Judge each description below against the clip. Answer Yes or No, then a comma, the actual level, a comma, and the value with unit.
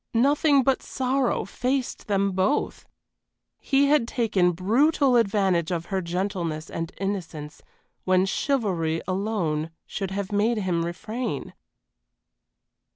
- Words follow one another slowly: Yes, slow, 110 wpm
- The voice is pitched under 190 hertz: No, high, 195 Hz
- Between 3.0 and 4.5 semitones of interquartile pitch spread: No, wide, 5.5 semitones